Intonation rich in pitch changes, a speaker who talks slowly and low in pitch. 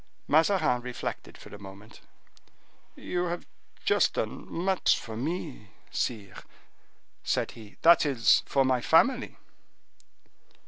Yes: wide, 7.3 semitones; slow, 110 wpm; low, 130 Hz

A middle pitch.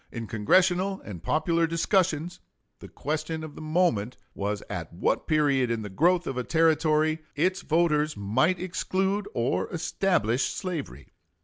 Yes: medium, 155 Hz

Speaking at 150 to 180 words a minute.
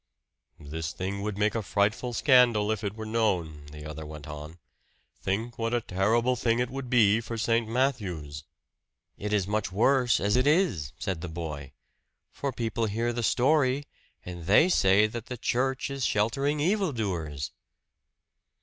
Yes: average, 165 wpm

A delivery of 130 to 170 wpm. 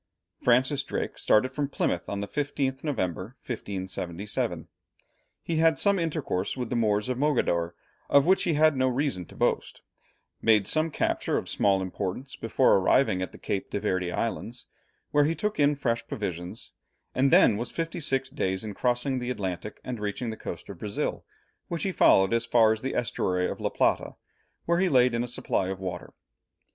No: average, 185 wpm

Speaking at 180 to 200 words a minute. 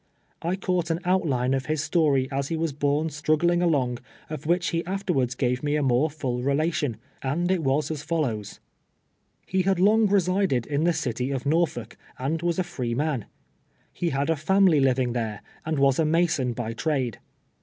Yes: average, 185 wpm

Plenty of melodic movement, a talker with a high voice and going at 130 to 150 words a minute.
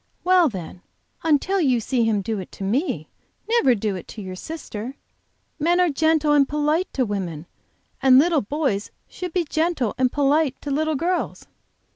No: wide, 6.5 semitones; very high, 280 Hz; average, 170 wpm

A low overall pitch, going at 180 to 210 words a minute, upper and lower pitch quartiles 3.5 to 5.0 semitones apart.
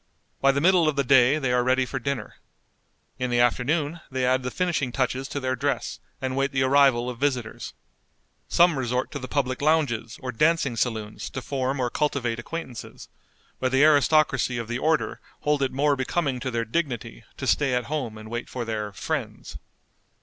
No: low, 130 Hz; average, 190 wpm; average, 2.8 semitones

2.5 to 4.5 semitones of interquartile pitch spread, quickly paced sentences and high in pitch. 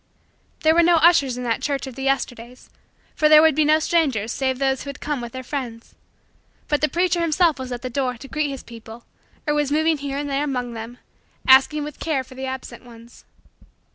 Yes: average, 3.4 semitones; fast, 220 wpm; very high, 275 Hz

